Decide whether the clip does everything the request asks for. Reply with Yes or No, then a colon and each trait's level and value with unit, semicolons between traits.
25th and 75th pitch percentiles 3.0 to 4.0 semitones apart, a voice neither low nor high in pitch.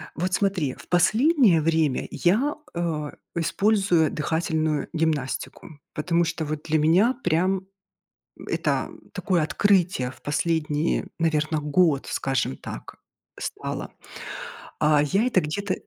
Yes: average, 3.4 semitones; medium, 165 Hz